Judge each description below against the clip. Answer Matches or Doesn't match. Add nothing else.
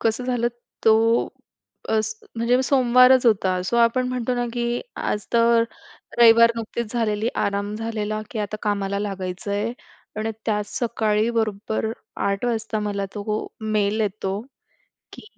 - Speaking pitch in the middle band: Doesn't match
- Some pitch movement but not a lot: Doesn't match